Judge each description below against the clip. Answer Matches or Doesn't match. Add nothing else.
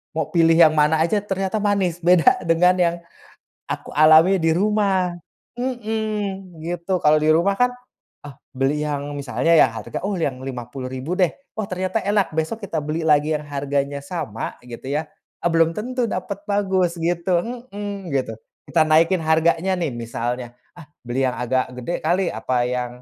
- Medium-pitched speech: Matches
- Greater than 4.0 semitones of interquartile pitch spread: Matches